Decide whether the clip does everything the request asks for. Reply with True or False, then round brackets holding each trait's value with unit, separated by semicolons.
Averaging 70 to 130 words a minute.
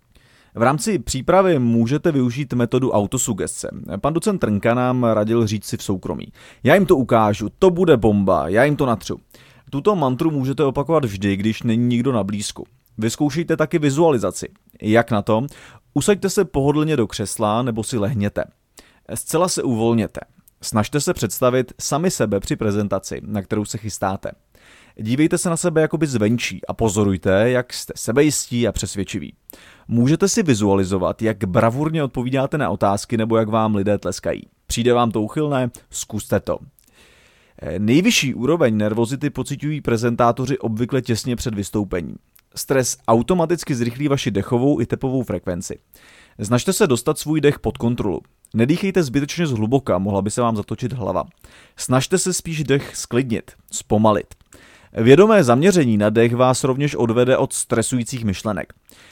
False (150 wpm)